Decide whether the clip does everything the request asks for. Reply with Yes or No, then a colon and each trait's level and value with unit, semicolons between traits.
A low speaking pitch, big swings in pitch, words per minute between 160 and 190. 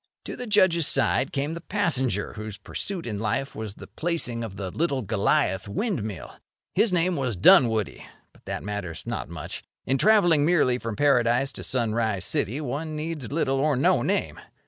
Yes: low, 130 Hz; wide, 7.0 semitones; average, 170 wpm